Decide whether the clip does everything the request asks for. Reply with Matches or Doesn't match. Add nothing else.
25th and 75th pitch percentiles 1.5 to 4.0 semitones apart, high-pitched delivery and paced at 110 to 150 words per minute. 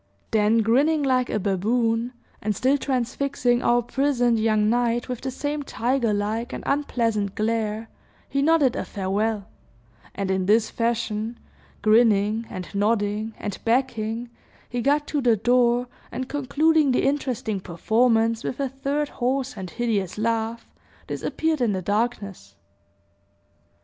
Matches